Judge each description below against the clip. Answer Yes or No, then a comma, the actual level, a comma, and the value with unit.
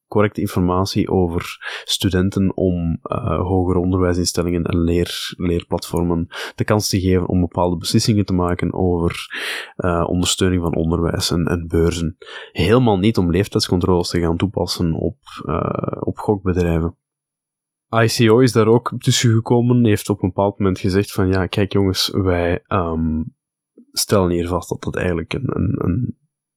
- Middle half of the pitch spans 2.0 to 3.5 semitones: Yes, average, 3.2 semitones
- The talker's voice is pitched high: No, very low, 95 Hz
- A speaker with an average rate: Yes, average, 150 wpm